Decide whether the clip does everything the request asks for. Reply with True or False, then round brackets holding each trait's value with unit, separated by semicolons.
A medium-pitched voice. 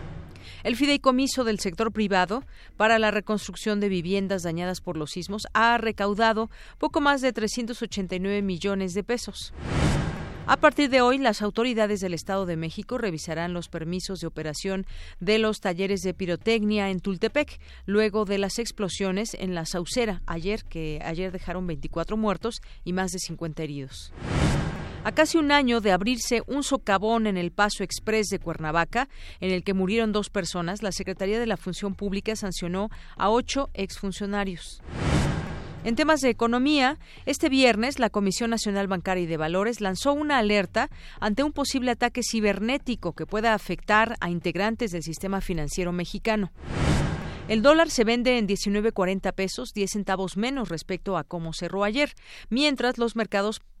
False (205 Hz)